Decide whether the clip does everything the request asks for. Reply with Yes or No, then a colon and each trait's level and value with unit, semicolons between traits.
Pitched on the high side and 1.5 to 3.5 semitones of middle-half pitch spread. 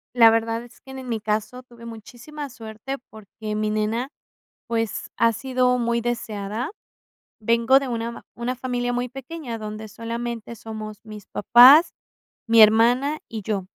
Yes: high, 230 Hz; narrow, 2.4 semitones